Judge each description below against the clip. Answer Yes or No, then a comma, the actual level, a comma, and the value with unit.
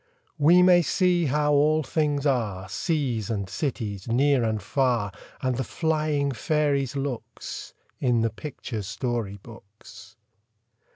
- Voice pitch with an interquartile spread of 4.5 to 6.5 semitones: Yes, average, 5.0 semitones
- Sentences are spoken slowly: Yes, slow, 125 wpm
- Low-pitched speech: Yes, low, 130 Hz